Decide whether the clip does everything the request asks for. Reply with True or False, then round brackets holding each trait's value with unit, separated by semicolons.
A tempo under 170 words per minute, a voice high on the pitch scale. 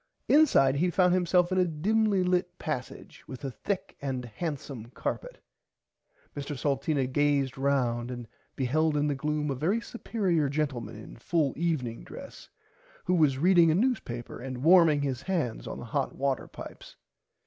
False (160 wpm; 150 Hz)